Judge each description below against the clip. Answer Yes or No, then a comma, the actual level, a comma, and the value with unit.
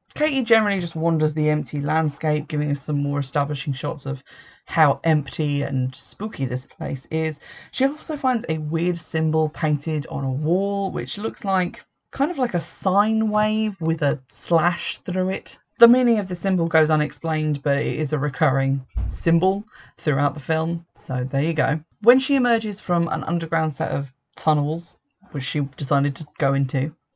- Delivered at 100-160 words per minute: No, average, 175 wpm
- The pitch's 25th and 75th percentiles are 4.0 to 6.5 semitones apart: Yes, average, 4.6 semitones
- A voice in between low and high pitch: Yes, medium, 160 Hz